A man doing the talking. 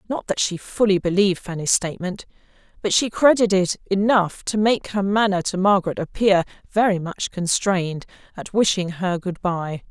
No: female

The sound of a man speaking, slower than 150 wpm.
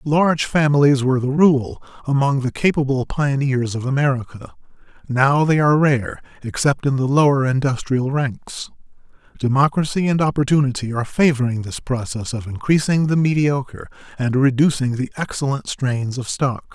Yes: male; average, 140 wpm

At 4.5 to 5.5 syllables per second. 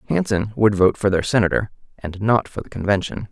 No: 5.7 syllables/s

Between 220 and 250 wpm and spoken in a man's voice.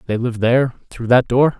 Yes: fast, 225 wpm; male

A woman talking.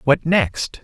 No: male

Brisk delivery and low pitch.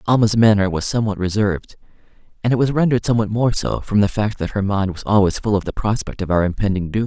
Yes: fast, 240 wpm; low, 105 Hz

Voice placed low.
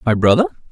Yes: low, 120 Hz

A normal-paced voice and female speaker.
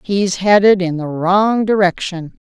Yes: average, 145 wpm; female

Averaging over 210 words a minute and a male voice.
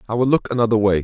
Yes: fast, 290 wpm; male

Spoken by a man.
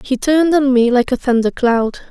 No: female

